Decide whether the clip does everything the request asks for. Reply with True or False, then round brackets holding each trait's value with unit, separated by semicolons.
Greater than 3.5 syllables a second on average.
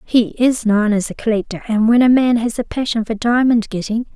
True (5.4 syllables/s)